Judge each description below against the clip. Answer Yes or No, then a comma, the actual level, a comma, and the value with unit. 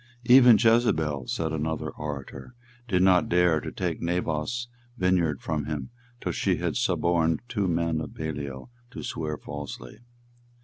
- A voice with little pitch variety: No, average, 3.4 semitones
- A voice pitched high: No, very low, 80 Hz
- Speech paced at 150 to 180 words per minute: No, average, 140 wpm